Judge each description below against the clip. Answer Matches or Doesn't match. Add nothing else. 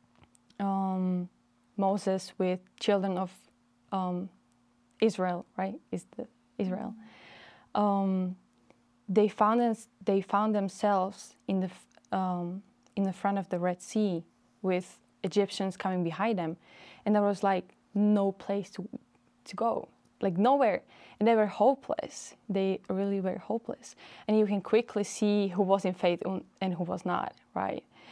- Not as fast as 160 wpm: Matches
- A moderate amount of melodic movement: Doesn't match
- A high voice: Matches